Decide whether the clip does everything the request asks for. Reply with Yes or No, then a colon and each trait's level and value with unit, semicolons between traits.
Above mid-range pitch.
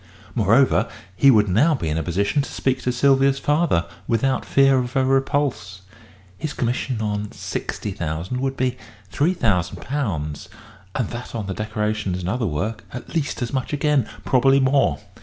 No: low, 125 Hz